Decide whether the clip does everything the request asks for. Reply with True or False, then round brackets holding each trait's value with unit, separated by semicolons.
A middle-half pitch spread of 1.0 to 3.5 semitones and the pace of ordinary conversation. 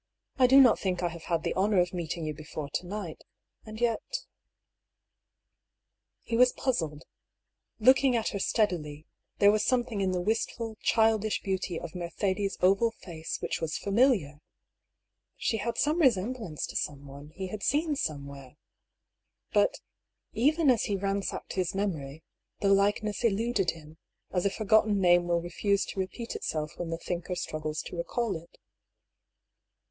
False (4.9 semitones; 160 wpm)